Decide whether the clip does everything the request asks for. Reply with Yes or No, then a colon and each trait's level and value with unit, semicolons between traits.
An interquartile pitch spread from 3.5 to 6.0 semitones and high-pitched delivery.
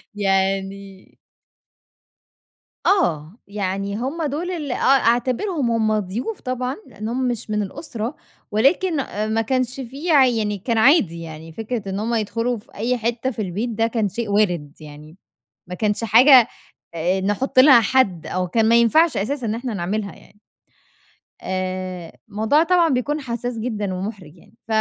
Yes: average, 4.7 semitones; high, 225 Hz